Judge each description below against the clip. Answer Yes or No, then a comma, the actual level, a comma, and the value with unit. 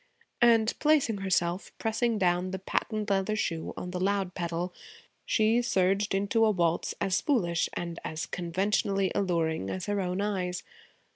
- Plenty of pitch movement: No, average, 3.0 semitones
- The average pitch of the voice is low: No, high, 190 Hz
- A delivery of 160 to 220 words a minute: No, average, 150 wpm